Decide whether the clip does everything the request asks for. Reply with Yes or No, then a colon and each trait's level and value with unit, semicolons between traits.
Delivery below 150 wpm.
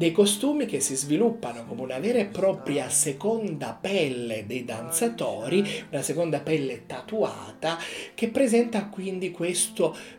Yes: average, 130 wpm